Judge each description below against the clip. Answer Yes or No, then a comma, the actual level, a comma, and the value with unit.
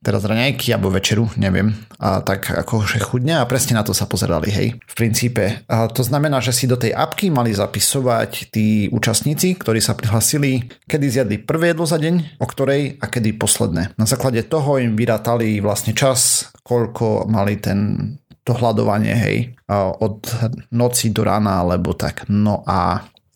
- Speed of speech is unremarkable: No, fast, 170 wpm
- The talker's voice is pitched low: Yes, low, 115 Hz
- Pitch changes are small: No, average, 3.6 semitones